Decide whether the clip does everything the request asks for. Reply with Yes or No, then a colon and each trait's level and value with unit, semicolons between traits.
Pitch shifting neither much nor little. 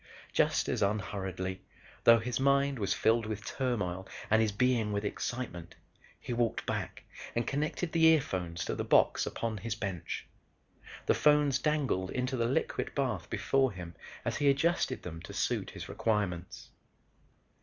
No: wide, 5.8 semitones